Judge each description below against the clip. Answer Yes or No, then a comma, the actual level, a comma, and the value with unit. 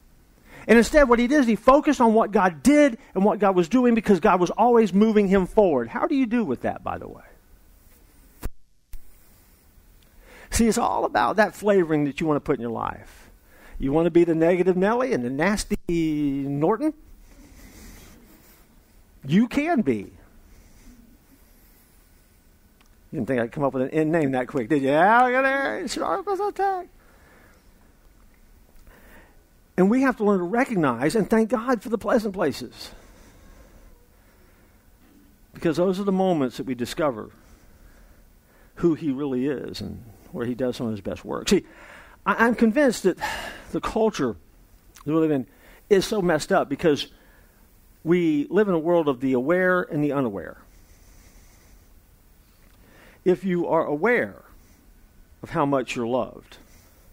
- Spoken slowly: No, average, 155 wpm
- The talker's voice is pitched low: No, medium, 150 Hz